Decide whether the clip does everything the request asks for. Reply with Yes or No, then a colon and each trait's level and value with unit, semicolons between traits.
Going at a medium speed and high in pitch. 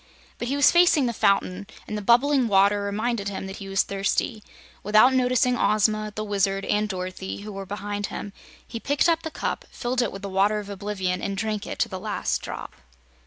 No: fast, 210 wpm; high, 210 Hz